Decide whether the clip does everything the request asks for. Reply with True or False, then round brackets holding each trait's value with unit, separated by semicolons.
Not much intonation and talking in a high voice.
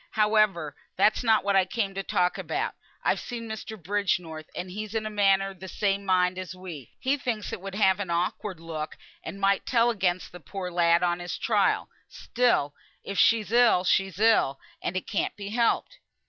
False (3.1 semitones; 195 Hz)